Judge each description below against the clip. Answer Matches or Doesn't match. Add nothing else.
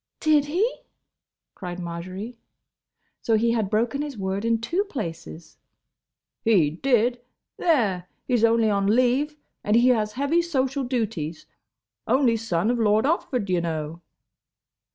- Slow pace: Matches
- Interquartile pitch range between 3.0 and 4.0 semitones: Doesn't match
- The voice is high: Matches